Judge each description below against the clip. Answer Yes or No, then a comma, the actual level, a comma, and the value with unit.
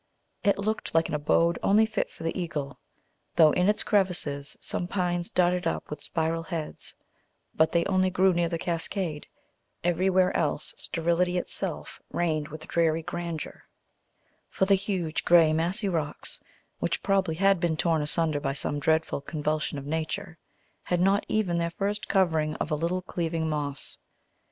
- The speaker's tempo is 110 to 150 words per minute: No, average, 160 wpm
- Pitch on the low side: No, medium, 170 Hz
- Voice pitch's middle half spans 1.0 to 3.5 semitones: Yes, average, 2.7 semitones